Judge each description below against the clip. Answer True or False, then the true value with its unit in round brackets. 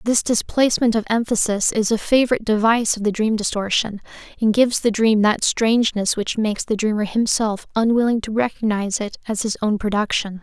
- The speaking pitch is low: False (220 Hz)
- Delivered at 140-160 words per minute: False (180 wpm)